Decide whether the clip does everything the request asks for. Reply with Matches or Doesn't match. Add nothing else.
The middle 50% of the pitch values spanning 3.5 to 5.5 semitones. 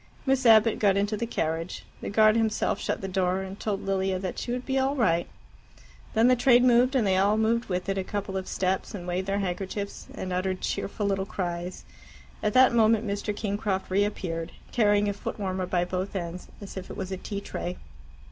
Doesn't match